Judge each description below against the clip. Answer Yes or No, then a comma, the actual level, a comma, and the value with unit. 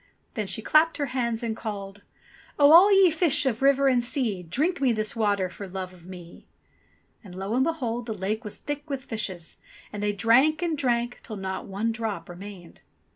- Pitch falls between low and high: No, high, 225 Hz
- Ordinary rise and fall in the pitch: No, wide, 5.7 semitones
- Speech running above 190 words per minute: Yes, average, 200 wpm